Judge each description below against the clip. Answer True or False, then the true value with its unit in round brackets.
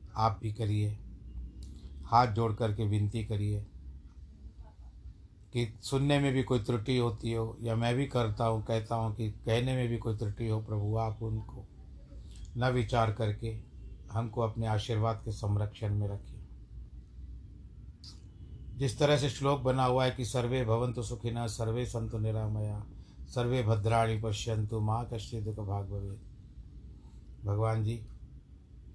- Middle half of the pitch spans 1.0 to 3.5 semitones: True (2.8 semitones)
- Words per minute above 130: True (140 wpm)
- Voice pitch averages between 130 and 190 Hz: False (110 Hz)